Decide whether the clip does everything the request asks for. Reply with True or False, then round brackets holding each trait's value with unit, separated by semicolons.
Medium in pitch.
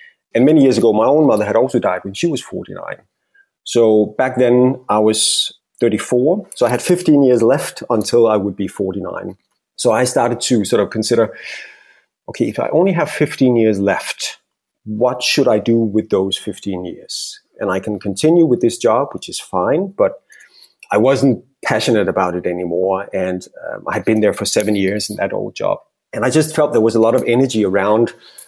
False (115 Hz)